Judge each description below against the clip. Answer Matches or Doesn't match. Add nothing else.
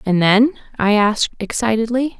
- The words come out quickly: Doesn't match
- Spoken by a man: Doesn't match